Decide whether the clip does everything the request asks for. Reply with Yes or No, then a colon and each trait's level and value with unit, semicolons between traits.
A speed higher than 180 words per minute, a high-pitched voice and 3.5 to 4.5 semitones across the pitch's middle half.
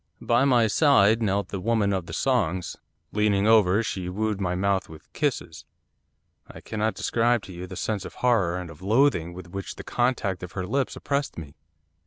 No: average, 190 wpm; low, 100 Hz; average, 3.9 semitones